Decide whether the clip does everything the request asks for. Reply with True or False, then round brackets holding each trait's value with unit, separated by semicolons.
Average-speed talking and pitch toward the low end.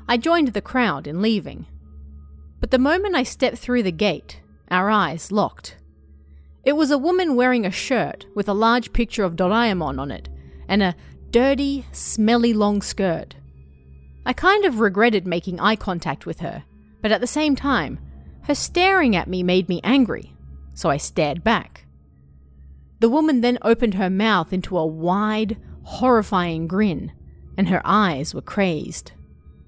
False (160 wpm; 190 Hz)